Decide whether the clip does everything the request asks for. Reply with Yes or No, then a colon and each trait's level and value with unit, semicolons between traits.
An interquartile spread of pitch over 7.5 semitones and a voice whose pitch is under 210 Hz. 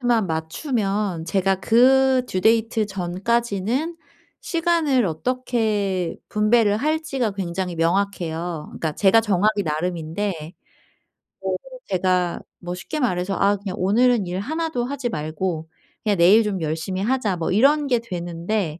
No: average, 5.3 semitones; high, 200 Hz